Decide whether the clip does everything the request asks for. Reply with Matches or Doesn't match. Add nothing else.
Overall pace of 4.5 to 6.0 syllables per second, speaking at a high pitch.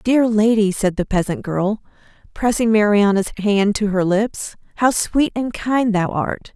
Doesn't match